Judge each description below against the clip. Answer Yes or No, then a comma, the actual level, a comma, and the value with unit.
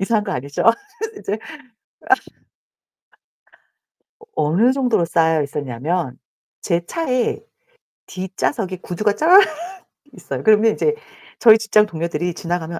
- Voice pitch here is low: No, high, 190 Hz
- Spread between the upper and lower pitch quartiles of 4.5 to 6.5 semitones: Yes, average, 5.2 semitones